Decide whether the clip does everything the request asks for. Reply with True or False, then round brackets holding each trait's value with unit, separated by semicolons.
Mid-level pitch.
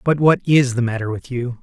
False (130 Hz)